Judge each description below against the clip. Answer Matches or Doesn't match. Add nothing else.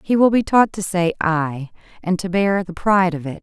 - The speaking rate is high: Matches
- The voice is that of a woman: Matches